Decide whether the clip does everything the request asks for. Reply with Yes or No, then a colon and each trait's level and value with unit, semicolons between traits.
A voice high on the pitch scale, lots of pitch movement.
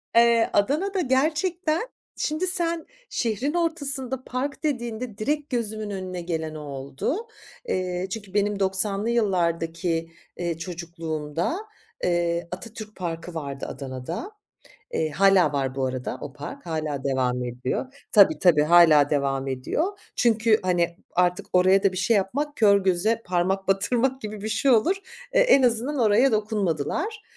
Yes: high, 195 Hz; wide, 7.2 semitones